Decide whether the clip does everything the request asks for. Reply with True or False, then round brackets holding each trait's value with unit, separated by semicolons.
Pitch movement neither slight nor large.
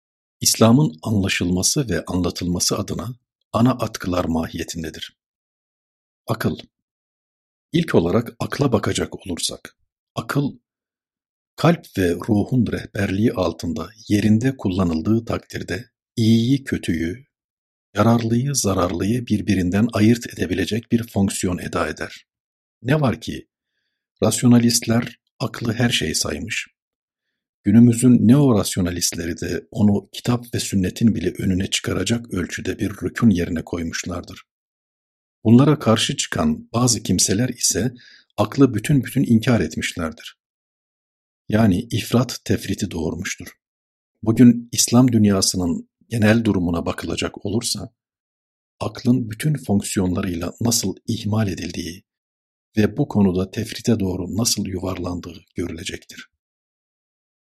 True (4.6 semitones)